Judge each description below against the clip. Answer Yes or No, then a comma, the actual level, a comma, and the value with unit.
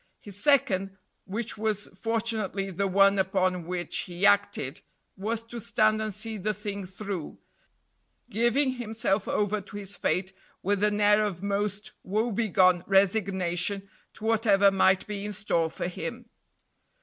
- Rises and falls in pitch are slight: Yes, narrow, 2.2 semitones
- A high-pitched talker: Yes, high, 200 Hz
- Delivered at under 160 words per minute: Yes, average, 140 wpm